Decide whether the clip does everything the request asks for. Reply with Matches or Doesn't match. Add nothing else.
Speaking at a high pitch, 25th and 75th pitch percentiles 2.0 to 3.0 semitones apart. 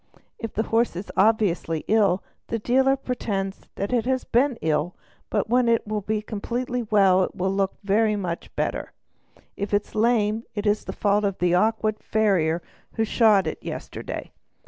Matches